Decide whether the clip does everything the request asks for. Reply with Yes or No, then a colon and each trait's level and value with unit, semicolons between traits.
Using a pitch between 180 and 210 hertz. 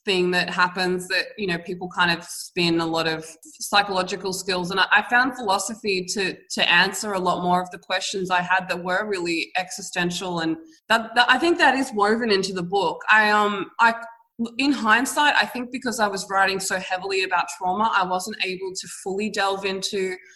Yes: high, 190 Hz